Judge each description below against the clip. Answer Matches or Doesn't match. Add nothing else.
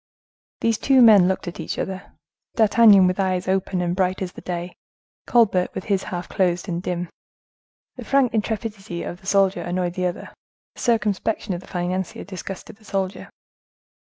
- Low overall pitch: Doesn't match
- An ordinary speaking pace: Matches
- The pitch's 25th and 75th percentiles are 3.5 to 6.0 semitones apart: Doesn't match